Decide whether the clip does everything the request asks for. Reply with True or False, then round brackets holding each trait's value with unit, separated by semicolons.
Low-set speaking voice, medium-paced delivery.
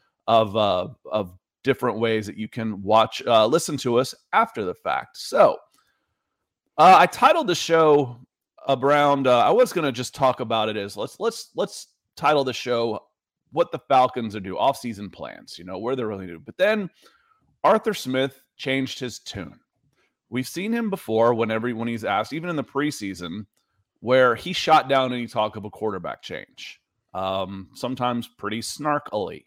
True (125 Hz; 175 wpm)